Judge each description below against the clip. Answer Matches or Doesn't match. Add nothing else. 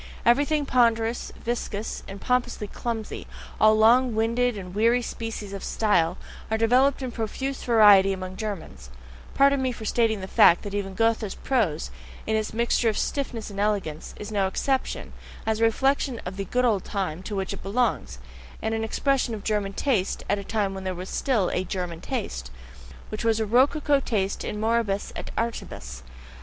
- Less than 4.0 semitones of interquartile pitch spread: Matches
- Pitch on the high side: Matches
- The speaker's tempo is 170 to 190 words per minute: Matches